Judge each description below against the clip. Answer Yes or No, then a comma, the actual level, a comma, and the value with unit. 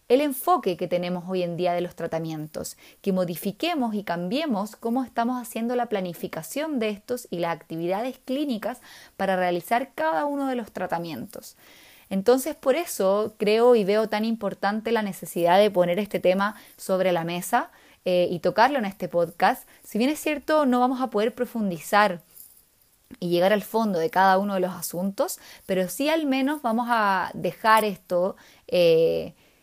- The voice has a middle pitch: No, high, 205 Hz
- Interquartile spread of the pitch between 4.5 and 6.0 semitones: Yes, wide, 5.4 semitones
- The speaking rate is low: No, average, 170 wpm